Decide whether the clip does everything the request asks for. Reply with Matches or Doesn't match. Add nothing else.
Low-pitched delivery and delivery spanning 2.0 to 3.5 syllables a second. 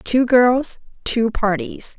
Doesn't match